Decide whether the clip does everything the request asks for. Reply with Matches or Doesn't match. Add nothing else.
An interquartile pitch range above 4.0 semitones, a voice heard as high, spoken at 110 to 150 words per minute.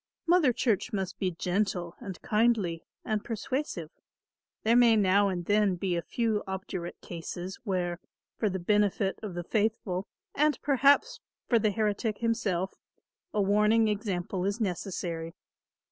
Doesn't match